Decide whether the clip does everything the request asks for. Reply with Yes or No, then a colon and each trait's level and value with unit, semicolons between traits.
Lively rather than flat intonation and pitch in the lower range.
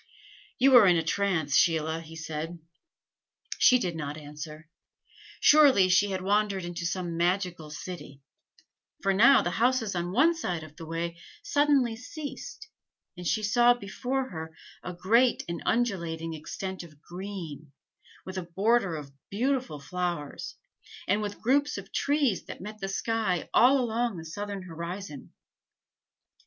No: wide, 5.8 semitones; medium, 185 Hz